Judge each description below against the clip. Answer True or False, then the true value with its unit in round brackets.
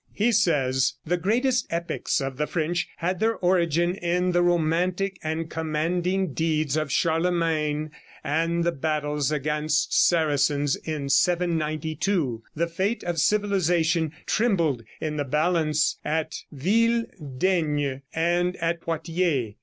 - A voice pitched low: False (165 Hz)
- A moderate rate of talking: False (120 wpm)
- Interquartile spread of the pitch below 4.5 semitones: True (2.7 semitones)